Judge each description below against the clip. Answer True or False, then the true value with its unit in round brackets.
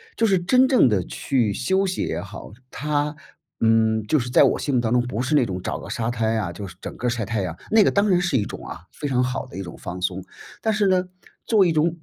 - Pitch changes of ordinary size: False (8.3 semitones)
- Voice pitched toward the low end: True (125 Hz)